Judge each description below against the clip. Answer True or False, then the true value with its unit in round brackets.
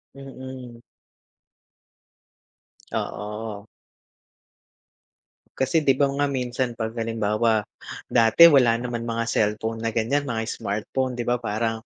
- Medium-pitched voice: False (115 Hz)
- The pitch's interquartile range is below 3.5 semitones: True (2.7 semitones)